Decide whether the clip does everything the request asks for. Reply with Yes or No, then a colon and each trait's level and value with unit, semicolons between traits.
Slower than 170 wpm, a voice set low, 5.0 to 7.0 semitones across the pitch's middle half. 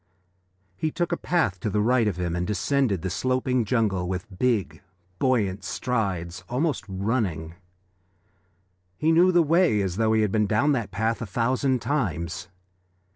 Yes: average, 160 wpm; low, 110 Hz; wide, 5.5 semitones